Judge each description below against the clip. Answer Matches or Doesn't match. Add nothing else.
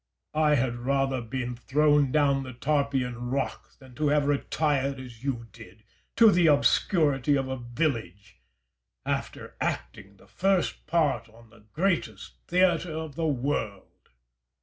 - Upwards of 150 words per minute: Doesn't match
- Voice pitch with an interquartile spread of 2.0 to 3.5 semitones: Doesn't match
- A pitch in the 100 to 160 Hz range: Matches